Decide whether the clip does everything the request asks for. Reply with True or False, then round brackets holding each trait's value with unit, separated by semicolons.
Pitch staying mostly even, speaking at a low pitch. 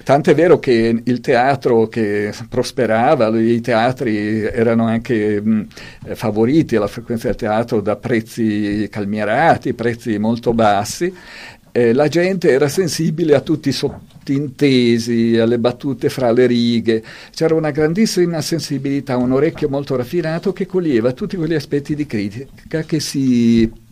False (4.9 semitones; 120 Hz)